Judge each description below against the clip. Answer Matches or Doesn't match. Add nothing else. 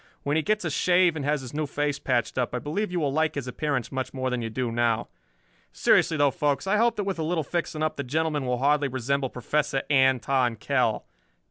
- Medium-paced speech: Doesn't match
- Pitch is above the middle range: Doesn't match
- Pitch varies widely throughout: Doesn't match